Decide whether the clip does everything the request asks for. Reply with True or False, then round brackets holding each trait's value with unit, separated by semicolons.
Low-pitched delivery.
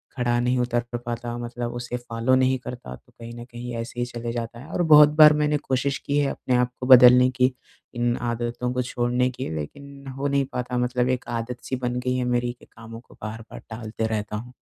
True (125 Hz)